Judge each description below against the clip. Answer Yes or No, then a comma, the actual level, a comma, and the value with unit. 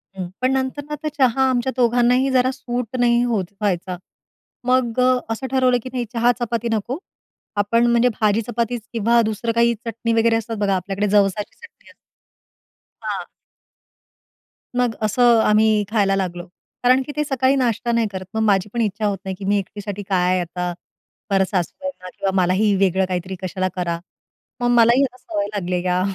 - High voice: Yes, high, 225 Hz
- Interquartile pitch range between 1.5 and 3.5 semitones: No, average, 4.0 semitones